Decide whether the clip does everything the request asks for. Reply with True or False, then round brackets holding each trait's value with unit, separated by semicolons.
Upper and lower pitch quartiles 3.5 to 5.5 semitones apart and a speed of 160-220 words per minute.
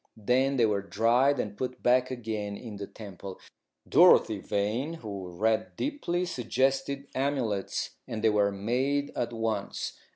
False (4.5 semitones; 140 wpm)